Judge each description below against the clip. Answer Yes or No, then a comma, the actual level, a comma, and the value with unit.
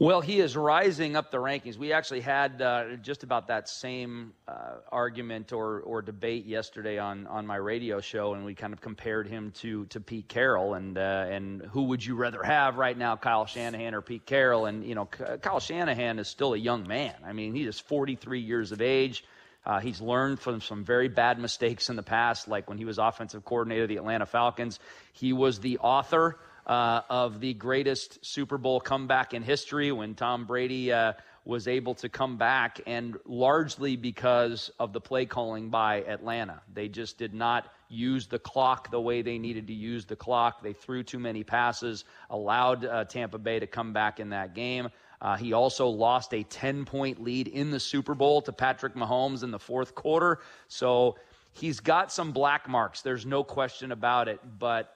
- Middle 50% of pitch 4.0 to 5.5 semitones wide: No, average, 2.7 semitones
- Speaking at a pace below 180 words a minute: No, average, 200 wpm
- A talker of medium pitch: No, low, 120 Hz